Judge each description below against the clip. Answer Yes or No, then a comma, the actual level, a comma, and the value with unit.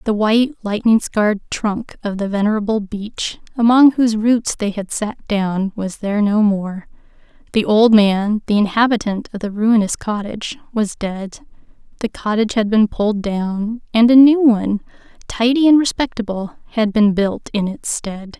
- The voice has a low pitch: No, high, 215 Hz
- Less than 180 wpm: Yes, average, 165 wpm